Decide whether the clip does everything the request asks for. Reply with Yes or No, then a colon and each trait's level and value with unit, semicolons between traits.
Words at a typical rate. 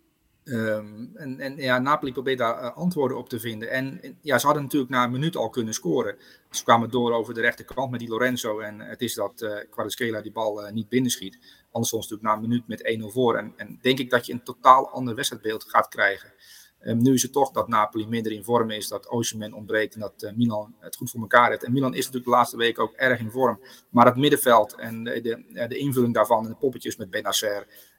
No: fast, 240 wpm